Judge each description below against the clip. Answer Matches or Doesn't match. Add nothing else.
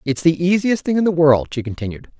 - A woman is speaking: Doesn't match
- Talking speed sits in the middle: Doesn't match